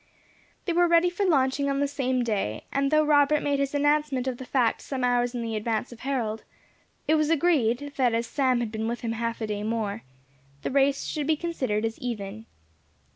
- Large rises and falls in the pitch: No, average, 4.1 semitones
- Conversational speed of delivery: No, fast, 210 wpm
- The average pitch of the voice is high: Yes, very high, 260 Hz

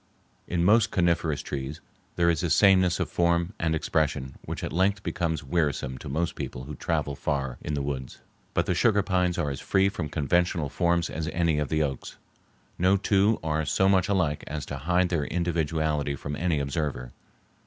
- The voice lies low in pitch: Yes, very low, 80 Hz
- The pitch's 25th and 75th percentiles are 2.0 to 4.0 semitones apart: Yes, average, 3.5 semitones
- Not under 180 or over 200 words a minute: Yes, average, 185 wpm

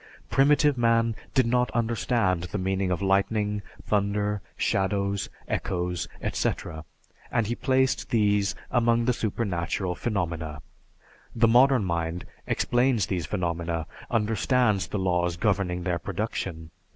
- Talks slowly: Yes, slow, 115 wpm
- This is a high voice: No, low, 100 Hz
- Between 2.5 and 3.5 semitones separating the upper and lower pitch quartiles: No, average, 4.7 semitones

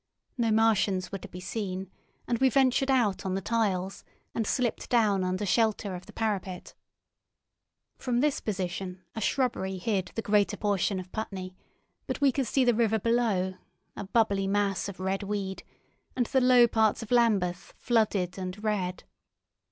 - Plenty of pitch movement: No, average, 3.5 semitones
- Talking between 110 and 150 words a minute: No, average, 165 wpm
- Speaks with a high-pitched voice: Yes, high, 205 Hz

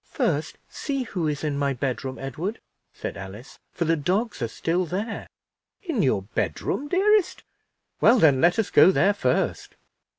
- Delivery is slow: No, average, 160 wpm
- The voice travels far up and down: Yes, wide, 8.5 semitones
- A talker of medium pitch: Yes, medium, 170 Hz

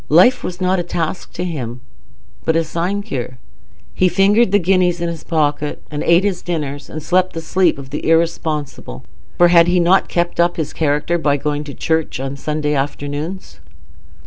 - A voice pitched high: No, medium, 165 Hz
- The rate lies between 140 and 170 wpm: No, average, 185 wpm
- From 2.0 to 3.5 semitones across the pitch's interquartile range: Yes, average, 3.2 semitones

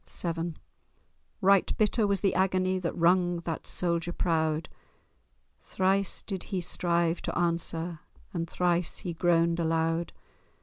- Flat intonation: Yes, narrow, 1.8 semitones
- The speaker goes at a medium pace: No, slow, 125 wpm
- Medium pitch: Yes, medium, 175 Hz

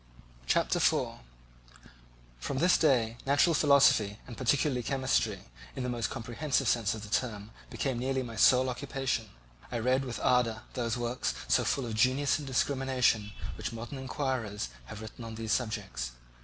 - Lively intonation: No, average, 3.0 semitones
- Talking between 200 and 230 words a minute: No, average, 155 wpm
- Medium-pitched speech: No, low, 125 Hz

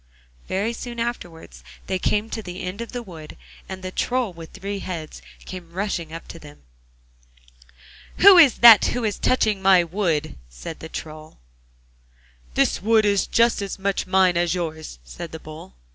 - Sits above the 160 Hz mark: Yes, medium, 185 Hz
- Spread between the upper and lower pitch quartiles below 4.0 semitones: No, average, 4.6 semitones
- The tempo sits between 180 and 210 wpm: No, average, 170 wpm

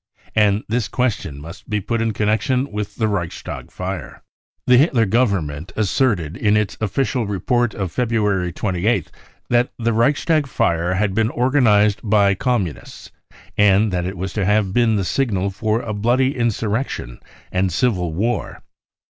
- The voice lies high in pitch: No, low, 105 Hz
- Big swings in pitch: No, average, 3.9 semitones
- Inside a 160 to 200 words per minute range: No, average, 150 wpm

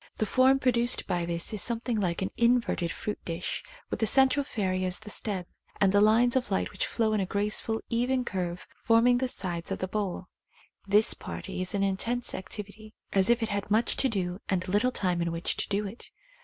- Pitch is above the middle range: Yes, high, 210 Hz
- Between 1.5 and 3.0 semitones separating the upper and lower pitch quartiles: No, average, 4.0 semitones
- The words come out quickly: Yes, fast, 215 wpm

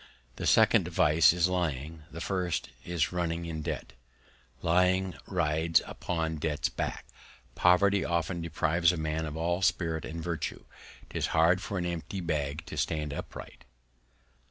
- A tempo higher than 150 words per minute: No, average, 145 wpm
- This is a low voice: Yes, very low, 85 Hz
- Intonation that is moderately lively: No, narrow, 2.0 semitones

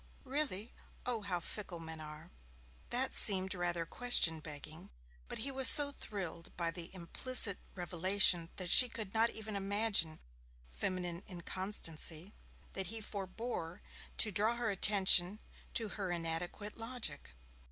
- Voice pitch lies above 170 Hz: Yes, high, 190 Hz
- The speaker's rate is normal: No, slow, 130 wpm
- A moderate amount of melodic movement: Yes, average, 4.5 semitones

